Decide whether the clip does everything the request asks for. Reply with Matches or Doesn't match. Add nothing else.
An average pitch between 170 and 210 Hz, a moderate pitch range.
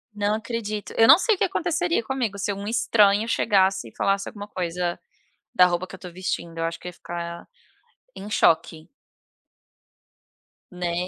Matches